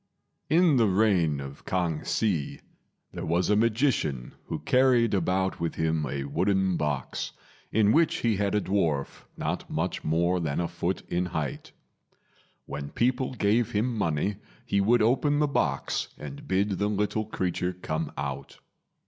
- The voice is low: Yes, very low, 95 Hz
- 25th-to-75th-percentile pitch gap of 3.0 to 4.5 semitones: No, wide, 5.6 semitones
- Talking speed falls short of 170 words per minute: Yes, average, 155 wpm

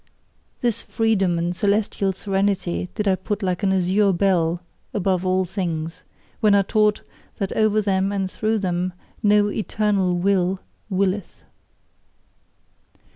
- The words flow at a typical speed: No, slow, 130 wpm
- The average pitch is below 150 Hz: No, high, 195 Hz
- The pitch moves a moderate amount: No, narrow, 2.1 semitones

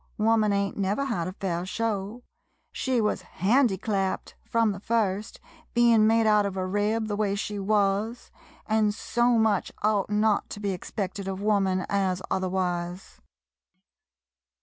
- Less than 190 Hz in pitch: No, high, 205 Hz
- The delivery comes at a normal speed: Yes, average, 150 wpm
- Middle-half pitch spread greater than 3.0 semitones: No, narrow, 2.4 semitones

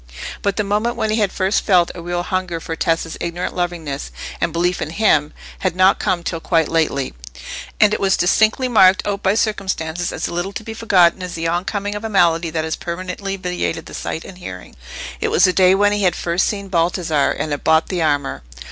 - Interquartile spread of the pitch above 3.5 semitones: No, average, 3.2 semitones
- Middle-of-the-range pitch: Yes, medium, 180 Hz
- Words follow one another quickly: Yes, fast, 215 wpm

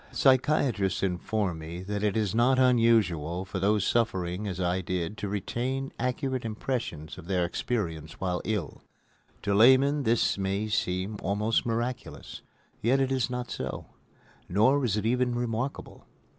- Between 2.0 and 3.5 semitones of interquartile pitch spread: No, average, 5.0 semitones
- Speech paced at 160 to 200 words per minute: No, average, 145 wpm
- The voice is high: No, low, 105 Hz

